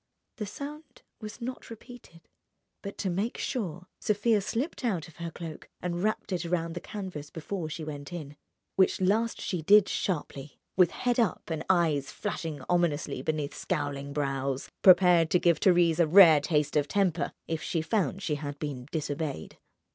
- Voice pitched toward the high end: No, medium, 170 Hz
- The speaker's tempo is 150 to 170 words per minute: Yes, average, 165 wpm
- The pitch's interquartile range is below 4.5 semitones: No, average, 4.8 semitones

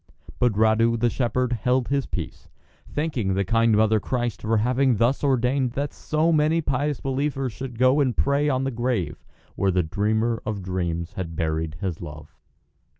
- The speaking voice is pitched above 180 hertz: No, low, 120 Hz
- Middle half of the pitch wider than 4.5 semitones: Yes, average, 5.2 semitones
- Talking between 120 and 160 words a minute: No, average, 175 wpm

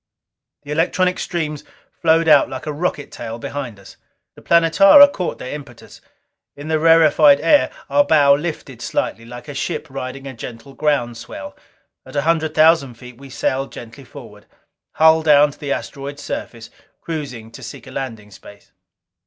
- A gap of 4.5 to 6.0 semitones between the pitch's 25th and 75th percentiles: No, average, 3.9 semitones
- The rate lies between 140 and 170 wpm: Yes, average, 165 wpm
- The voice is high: No, medium, 145 Hz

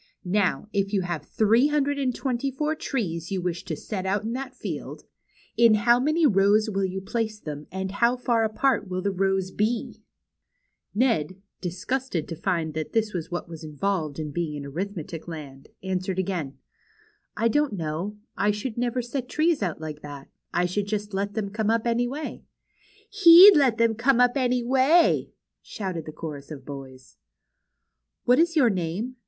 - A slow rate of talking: No, average, 185 wpm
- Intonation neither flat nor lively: No, wide, 6.0 semitones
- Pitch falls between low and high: No, high, 205 Hz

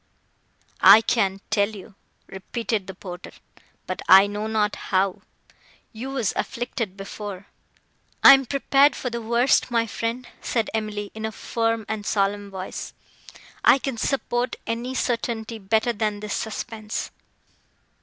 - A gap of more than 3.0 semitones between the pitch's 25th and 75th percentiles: No, narrow, 2.6 semitones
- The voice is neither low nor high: No, high, 220 Hz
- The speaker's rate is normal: No, slow, 130 wpm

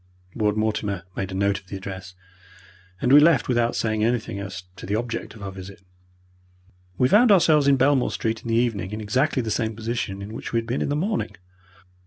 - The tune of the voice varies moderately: Yes, average, 4.1 semitones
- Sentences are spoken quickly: Yes, fast, 215 wpm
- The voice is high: No, low, 110 Hz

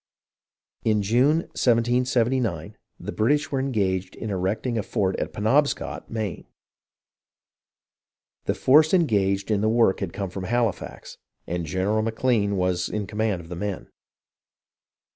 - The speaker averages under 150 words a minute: Yes, slow, 135 wpm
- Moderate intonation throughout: Yes, average, 4.1 semitones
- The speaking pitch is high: No, low, 110 Hz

